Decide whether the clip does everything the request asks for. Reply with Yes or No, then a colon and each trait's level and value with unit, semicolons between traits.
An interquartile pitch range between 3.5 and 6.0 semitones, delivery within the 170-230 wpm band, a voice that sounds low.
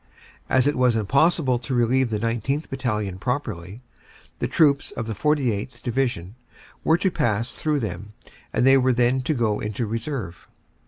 No: average, 4.0 semitones; average, 160 wpm; low, 120 Hz